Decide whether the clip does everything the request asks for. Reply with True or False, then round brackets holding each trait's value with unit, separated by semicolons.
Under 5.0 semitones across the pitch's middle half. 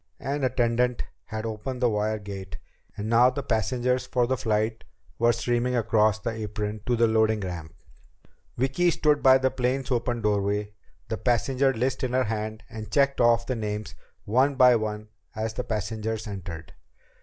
True (2.9 semitones)